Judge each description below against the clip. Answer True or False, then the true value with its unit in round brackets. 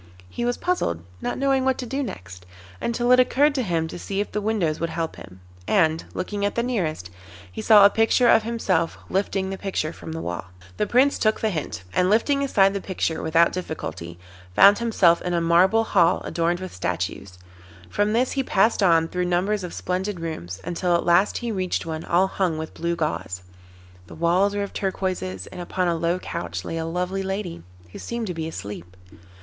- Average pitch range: True (4.5 semitones)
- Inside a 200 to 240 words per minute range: True (205 wpm)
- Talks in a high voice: False (180 Hz)